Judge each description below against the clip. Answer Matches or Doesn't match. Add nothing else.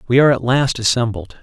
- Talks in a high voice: Doesn't match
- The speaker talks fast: Matches